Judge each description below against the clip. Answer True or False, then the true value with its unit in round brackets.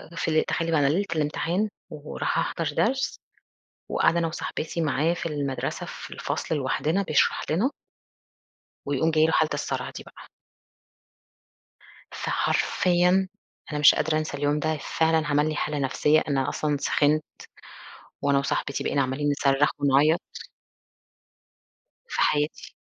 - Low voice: False (155 Hz)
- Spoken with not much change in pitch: True (2.1 semitones)